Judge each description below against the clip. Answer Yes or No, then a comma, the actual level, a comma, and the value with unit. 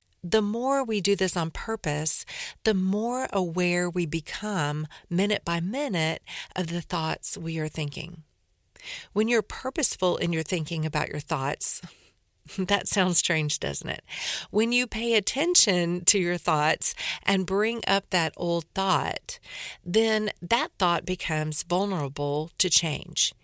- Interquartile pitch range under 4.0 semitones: No, average, 4.3 semitones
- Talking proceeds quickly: No, average, 140 wpm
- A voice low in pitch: No, medium, 180 Hz